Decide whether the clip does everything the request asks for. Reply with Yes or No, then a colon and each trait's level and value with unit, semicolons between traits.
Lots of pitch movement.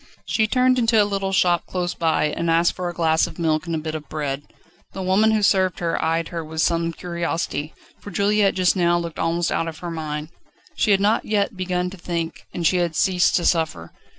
No: average, 2.8 semitones